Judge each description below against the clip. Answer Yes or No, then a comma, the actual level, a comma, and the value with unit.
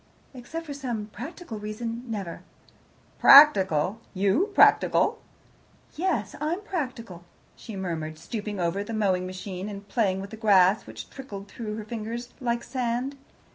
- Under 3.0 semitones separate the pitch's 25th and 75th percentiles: No, average, 4.3 semitones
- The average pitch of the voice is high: Yes, high, 215 Hz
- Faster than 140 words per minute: No, slow, 135 wpm